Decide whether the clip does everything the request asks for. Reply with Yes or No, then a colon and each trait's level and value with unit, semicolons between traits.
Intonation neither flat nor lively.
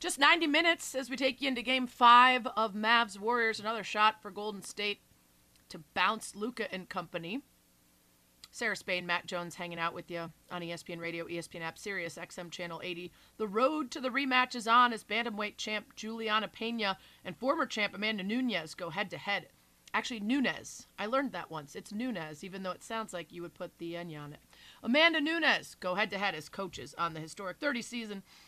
No: wide, 5.7 semitones